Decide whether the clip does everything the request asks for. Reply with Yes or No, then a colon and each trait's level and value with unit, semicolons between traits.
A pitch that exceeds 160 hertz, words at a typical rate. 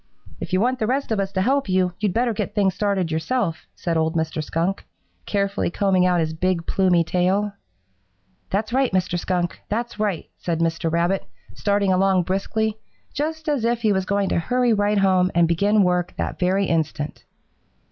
Yes: high, 190 Hz; average, 185 wpm